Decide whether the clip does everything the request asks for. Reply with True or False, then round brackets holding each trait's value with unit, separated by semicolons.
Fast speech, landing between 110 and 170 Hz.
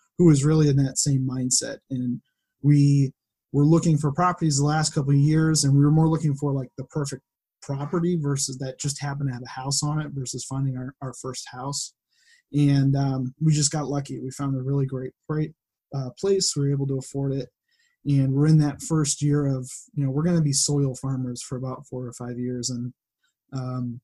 True (215 wpm; 140 Hz)